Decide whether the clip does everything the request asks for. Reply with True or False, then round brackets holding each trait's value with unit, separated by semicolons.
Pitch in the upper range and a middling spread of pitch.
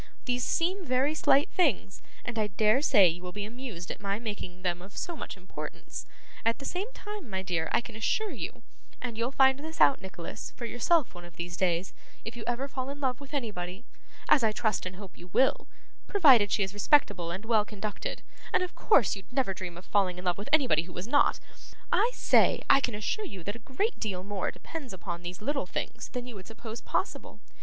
False (220 Hz; 6.2 semitones)